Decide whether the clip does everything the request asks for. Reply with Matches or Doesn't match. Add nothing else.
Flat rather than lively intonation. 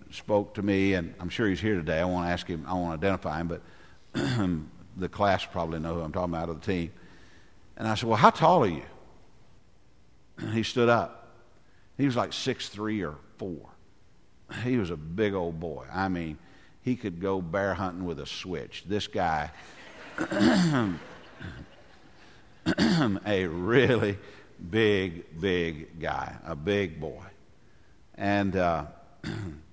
Doesn't match